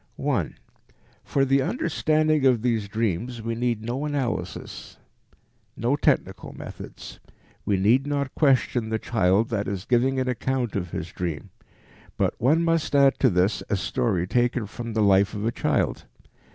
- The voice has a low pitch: Yes, low, 120 Hz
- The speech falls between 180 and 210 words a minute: No, average, 155 wpm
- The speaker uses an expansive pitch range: No, average, 4.7 semitones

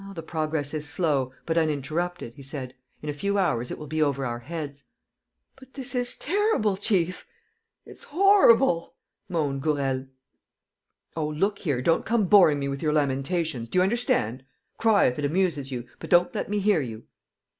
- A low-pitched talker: No, medium, 155 Hz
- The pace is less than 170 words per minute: No, average, 175 wpm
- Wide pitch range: Yes, wide, 5.9 semitones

